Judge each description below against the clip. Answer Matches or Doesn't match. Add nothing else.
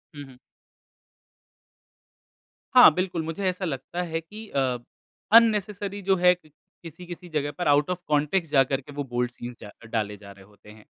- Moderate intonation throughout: Doesn't match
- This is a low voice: Doesn't match